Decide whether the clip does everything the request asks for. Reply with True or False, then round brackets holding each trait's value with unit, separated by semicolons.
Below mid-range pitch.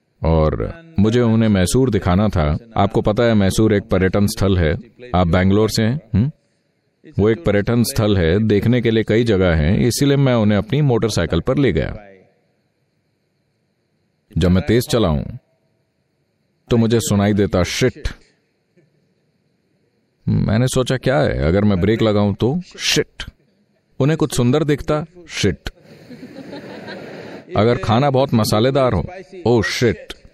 True (110 Hz)